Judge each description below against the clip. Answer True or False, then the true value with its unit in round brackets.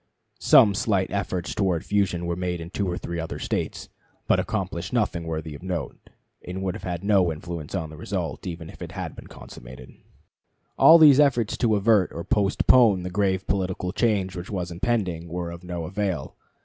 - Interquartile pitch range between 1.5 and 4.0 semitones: True (2.9 semitones)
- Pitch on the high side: False (90 Hz)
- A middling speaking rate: True (185 wpm)